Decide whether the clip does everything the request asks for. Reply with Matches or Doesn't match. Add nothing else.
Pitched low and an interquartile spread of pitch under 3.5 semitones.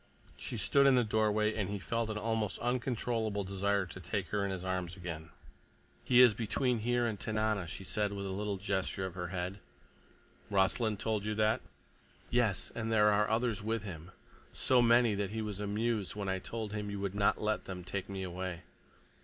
Matches